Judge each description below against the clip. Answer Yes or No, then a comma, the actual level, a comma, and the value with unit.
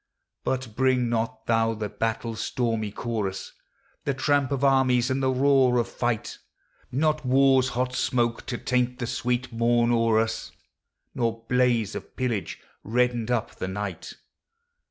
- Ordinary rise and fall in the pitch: No, narrow, 2.2 semitones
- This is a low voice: Yes, low, 120 Hz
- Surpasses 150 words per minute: No, average, 145 wpm